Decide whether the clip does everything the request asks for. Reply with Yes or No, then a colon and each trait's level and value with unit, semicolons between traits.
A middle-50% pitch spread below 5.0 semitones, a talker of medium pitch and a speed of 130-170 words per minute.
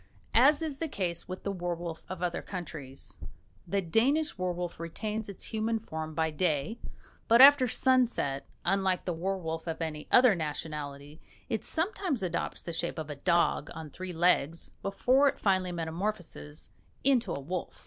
No: wide, 5.4 semitones; medium, 180 Hz; average, 160 wpm